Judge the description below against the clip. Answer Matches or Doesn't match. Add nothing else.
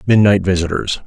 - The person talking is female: Doesn't match